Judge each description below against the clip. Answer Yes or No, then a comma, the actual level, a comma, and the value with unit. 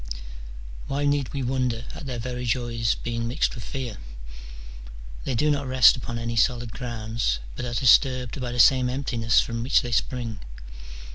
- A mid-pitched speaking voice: No, low, 120 Hz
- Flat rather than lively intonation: Yes, narrow, 1.9 semitones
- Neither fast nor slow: Yes, average, 165 wpm